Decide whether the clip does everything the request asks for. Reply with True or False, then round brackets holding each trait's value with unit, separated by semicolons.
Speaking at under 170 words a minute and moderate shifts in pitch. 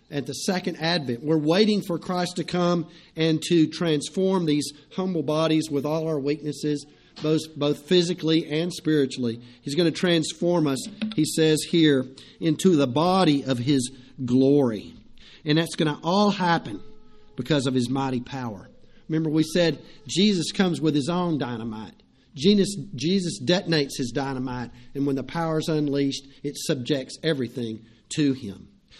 True (155 wpm; 3.7 semitones)